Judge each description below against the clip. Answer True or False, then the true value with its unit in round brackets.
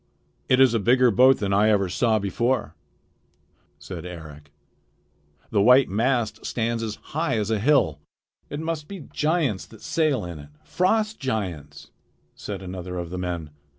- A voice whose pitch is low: True (110 Hz)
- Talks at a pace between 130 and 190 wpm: True (155 wpm)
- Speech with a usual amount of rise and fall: False (6.3 semitones)